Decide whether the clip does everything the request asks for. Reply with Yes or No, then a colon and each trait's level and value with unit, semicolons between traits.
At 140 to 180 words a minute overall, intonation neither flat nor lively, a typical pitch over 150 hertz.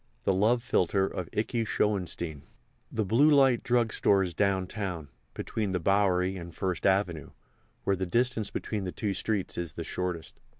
No: average, 165 wpm; average, 3.4 semitones; very low, 95 Hz